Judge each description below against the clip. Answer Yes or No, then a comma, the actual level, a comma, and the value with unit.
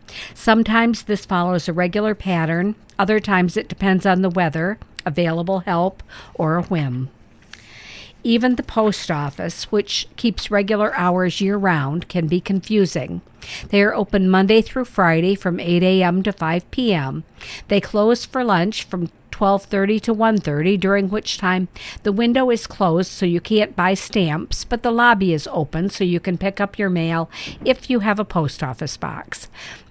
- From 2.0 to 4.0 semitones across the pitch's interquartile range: Yes, average, 3.5 semitones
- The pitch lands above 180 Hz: Yes, high, 190 Hz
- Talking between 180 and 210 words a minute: No, average, 165 wpm